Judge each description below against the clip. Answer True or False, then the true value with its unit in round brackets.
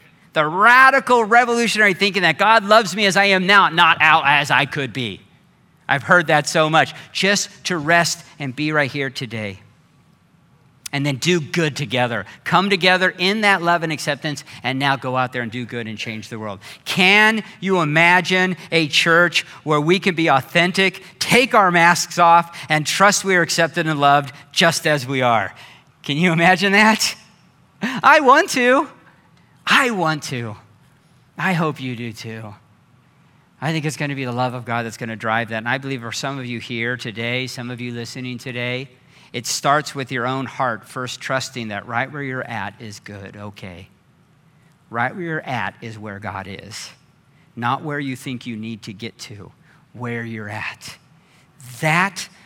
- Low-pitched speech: False (145 Hz)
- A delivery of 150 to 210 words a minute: True (185 wpm)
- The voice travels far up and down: True (5.8 semitones)